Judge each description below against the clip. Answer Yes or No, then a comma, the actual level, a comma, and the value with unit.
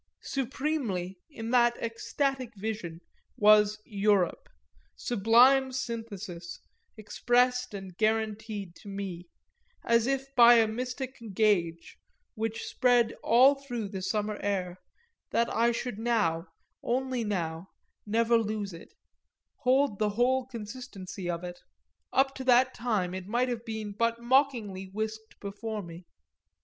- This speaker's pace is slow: Yes, slow, 125 wpm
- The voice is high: Yes, high, 220 Hz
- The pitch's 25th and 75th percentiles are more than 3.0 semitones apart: Yes, average, 3.7 semitones